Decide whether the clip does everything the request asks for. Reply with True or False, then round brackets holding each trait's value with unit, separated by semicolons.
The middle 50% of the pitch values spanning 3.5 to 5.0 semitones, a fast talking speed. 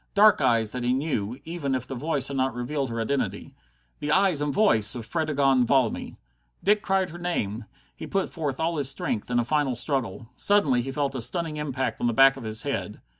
True (4.3 semitones; 215 wpm)